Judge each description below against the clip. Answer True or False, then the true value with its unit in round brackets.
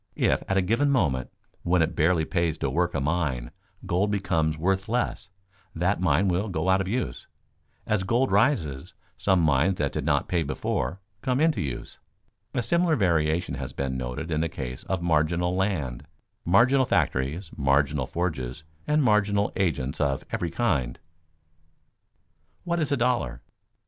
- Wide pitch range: True (5.8 semitones)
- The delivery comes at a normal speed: True (160 wpm)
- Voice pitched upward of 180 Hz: False (85 Hz)